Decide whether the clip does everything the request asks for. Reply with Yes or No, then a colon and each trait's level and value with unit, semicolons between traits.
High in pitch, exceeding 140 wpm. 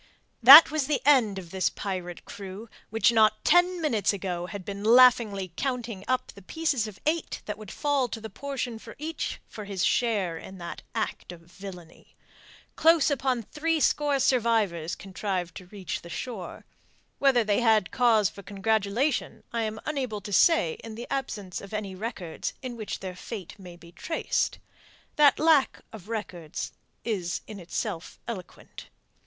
Yes: high, 215 Hz; average, 160 wpm